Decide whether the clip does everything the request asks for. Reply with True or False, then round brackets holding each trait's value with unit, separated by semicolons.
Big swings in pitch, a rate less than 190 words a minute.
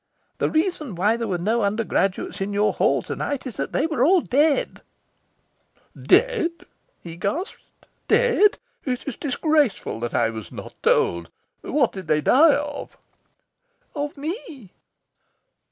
True (7.9 semitones; 140 wpm)